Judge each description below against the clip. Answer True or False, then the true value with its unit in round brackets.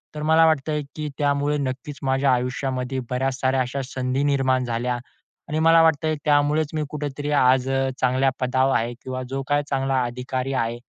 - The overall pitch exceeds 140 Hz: False (135 Hz)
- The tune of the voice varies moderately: False (2.2 semitones)